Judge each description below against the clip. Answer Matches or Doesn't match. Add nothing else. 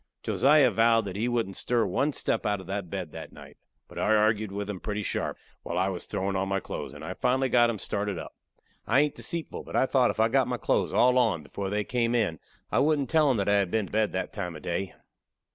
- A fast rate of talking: Matches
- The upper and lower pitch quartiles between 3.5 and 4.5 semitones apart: Matches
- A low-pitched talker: Matches